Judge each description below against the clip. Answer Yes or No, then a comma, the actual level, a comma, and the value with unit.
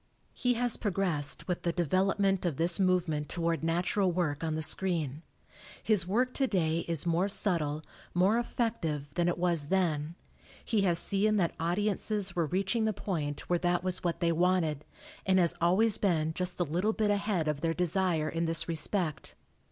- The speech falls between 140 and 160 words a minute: No, average, 175 wpm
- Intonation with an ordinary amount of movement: Yes, average, 3.1 semitones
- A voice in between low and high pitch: Yes, medium, 175 Hz